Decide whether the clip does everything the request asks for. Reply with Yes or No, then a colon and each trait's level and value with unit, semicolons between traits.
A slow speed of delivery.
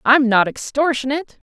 Yes: slow, 120 wpm